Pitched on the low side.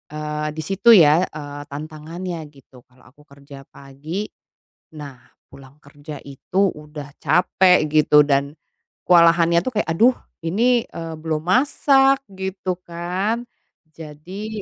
No: medium, 160 Hz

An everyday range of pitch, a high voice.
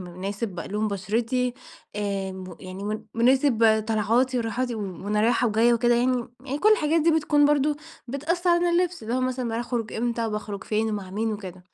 Yes: average, 3.6 semitones; high, 230 Hz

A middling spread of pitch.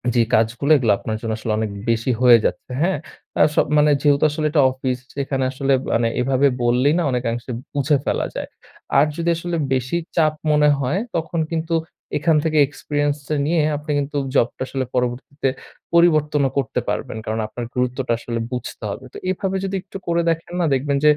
Yes: average, 3.8 semitones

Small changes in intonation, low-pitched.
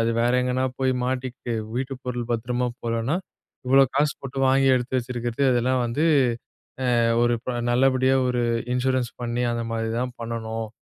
Yes: narrow, 1.7 semitones; low, 125 Hz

